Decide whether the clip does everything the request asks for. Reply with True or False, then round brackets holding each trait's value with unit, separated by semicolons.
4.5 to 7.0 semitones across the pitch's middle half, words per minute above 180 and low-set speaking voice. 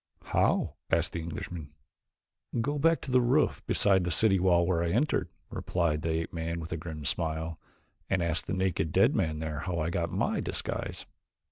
False (2.9 semitones; 190 wpm; 85 Hz)